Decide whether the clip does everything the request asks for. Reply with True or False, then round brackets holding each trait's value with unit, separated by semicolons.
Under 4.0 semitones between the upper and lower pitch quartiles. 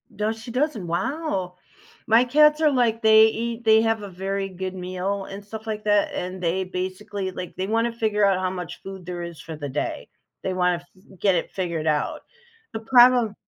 True (3.6 semitones)